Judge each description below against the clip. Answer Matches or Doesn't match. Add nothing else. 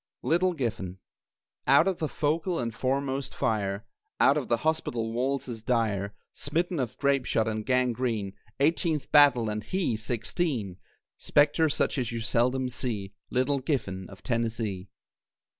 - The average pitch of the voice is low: Matches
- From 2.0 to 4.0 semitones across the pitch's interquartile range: Doesn't match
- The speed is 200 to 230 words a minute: Doesn't match